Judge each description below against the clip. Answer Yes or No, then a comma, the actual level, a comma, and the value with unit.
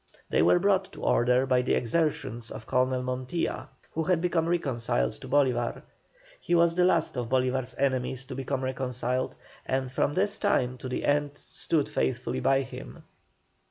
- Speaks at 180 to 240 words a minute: No, average, 165 wpm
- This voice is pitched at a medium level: No, low, 130 Hz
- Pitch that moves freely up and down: No, average, 3.6 semitones